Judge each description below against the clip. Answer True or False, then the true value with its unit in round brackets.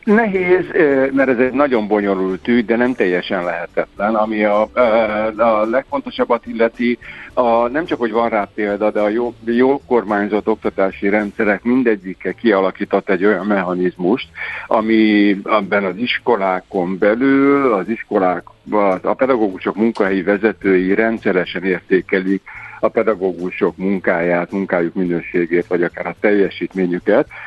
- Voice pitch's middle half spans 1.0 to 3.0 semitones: False (3.4 semitones)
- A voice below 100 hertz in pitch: False (105 Hz)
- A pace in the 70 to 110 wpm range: False (125 wpm)